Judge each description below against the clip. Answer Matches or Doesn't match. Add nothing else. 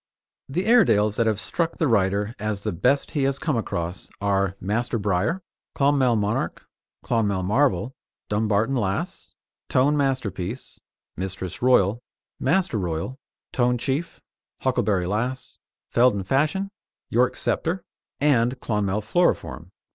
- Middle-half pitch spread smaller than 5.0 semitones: Doesn't match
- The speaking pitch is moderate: Doesn't match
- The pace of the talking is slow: Matches